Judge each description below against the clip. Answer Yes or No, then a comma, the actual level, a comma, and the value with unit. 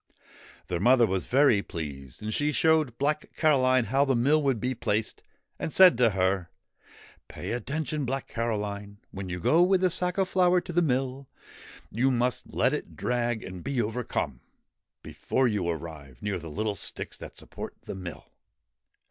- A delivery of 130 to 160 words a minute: No, average, 175 wpm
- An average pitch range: No, wide, 6.2 semitones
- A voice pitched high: No, low, 120 Hz